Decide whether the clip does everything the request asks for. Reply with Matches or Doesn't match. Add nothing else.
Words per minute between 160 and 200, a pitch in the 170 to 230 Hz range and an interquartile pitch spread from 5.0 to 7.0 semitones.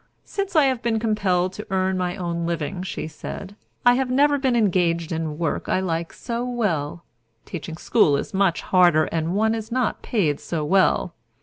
Matches